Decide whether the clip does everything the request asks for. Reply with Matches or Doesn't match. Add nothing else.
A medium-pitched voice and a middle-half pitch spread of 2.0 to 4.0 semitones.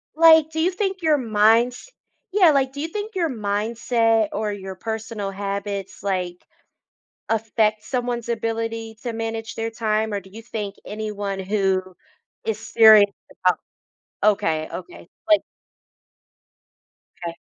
Doesn't match